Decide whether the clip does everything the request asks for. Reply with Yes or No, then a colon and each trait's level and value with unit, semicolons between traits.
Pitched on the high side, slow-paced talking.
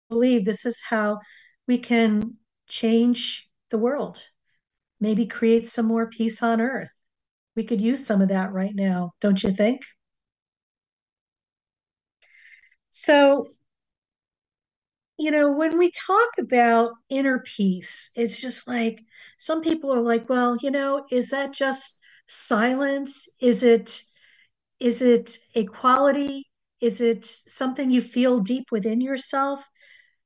Yes: high, 245 Hz; slow, 125 wpm